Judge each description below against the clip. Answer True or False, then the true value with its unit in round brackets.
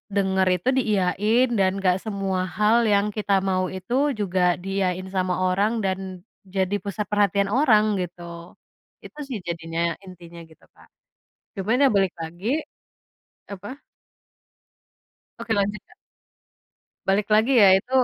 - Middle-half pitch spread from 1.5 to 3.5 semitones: True (2.6 semitones)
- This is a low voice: False (195 Hz)